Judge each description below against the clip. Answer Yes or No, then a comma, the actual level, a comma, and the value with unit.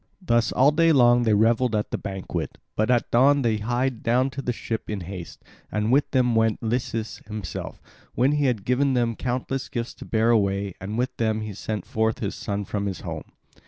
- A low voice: Yes, low, 115 Hz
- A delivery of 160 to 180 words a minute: No, fast, 205 wpm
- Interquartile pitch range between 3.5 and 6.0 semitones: No, average, 2.9 semitones